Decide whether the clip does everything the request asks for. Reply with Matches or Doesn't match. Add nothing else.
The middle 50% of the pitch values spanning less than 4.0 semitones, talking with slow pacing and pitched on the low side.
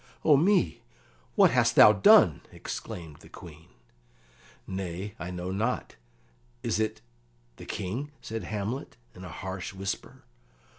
Matches